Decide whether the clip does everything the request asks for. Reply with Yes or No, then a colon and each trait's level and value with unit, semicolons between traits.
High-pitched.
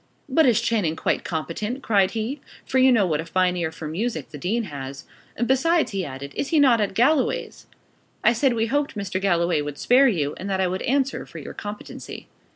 Yes: high, 205 Hz